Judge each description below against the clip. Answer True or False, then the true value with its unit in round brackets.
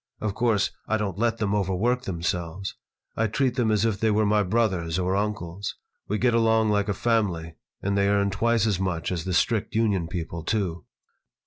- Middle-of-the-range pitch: False (100 Hz)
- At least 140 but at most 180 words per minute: False (195 wpm)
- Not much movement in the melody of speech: False (3.3 semitones)